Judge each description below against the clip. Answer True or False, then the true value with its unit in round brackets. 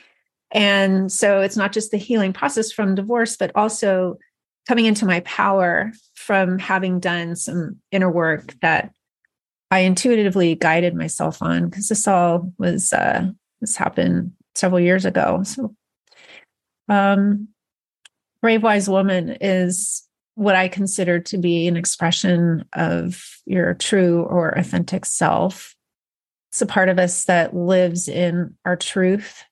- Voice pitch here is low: False (190 Hz)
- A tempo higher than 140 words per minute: False (135 wpm)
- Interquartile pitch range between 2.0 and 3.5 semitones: True (2.7 semitones)